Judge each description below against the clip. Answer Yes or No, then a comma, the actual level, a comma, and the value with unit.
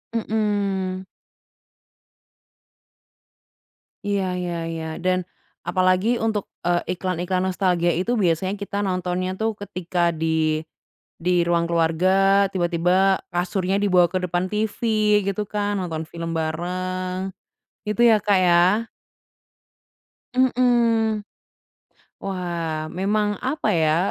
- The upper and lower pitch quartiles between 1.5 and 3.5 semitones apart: Yes, average, 2.7 semitones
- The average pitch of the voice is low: No, medium, 185 Hz